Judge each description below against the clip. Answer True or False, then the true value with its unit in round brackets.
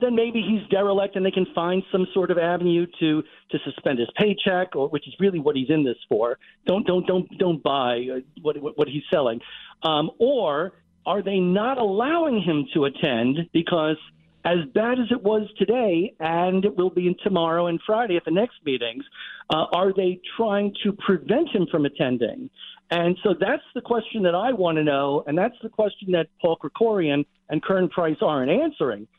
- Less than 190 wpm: False (195 wpm)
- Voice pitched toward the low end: False (180 Hz)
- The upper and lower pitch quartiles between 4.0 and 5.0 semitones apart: True (4.7 semitones)